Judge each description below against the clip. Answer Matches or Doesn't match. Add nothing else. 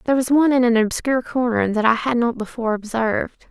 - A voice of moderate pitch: Doesn't match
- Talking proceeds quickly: Matches